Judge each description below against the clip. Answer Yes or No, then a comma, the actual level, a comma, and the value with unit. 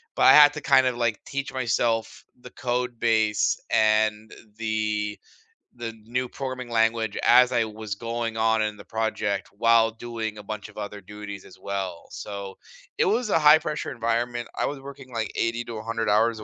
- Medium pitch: No, low, 115 Hz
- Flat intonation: Yes, narrow, 2.2 semitones